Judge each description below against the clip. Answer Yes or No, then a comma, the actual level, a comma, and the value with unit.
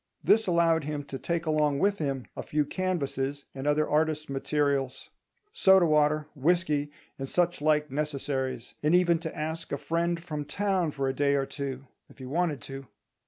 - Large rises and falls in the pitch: No, average, 3.2 semitones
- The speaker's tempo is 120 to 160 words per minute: No, average, 175 wpm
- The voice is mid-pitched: Yes, medium, 150 Hz